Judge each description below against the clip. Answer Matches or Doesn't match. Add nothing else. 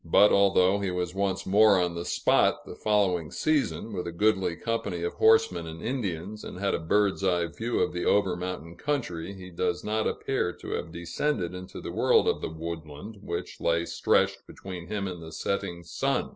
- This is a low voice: Matches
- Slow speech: Doesn't match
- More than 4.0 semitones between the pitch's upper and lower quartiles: Doesn't match